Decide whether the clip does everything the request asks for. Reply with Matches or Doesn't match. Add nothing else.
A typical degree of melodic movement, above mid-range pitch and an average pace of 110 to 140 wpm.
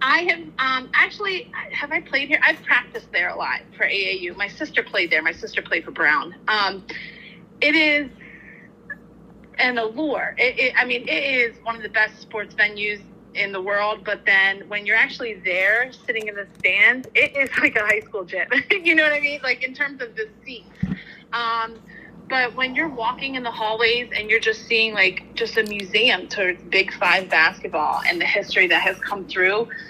Doesn't match